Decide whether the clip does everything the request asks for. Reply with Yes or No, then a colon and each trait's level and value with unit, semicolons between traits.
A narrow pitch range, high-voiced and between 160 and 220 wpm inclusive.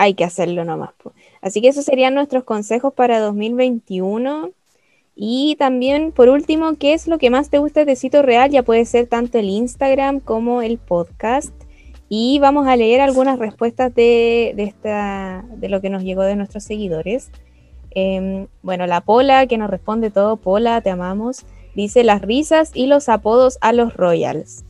No: average, 4.8 semitones; high, 230 Hz; average, 175 wpm